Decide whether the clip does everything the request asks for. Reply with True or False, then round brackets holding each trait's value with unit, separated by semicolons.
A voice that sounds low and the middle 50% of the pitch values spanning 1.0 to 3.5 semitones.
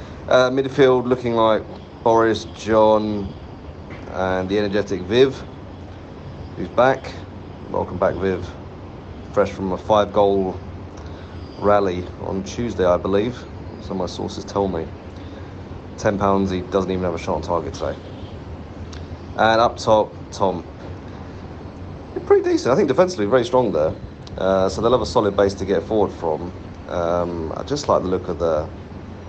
True (95 Hz; 2.7 semitones)